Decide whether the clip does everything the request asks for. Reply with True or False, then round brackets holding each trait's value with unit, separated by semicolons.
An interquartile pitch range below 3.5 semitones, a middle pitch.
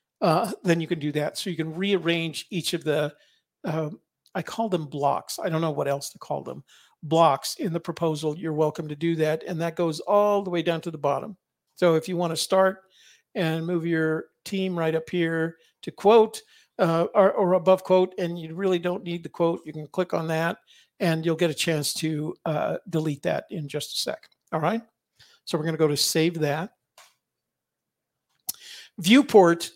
True (2.6 semitones; 170 Hz)